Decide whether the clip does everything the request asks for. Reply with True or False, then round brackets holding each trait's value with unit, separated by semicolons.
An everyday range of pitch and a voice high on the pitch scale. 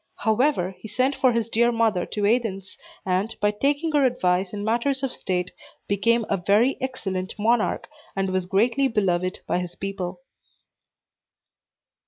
True (4.4 semitones; 210 Hz)